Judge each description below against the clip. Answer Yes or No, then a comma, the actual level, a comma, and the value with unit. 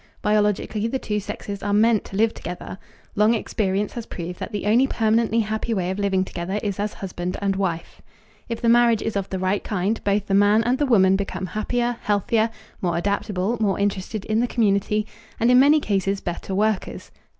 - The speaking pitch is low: No, high, 205 Hz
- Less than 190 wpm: No, average, 195 wpm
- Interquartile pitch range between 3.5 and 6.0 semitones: No, narrow, 2.5 semitones